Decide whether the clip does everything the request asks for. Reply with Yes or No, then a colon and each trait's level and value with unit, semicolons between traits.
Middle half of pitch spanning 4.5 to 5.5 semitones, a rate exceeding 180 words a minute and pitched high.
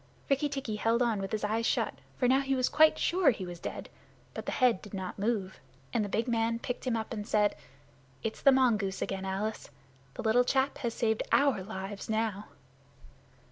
No: average, 3.5 semitones; average, 200 wpm; high, 225 Hz